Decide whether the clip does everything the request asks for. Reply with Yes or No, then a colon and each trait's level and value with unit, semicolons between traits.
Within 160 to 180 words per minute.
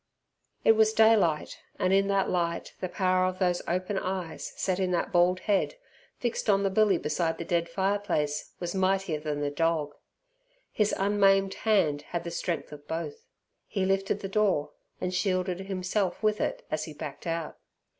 Yes: average, 175 wpm